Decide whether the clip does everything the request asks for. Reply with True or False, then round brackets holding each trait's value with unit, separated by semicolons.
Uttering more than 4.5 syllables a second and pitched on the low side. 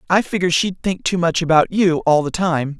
False (5.4 syllables/s; 170 Hz)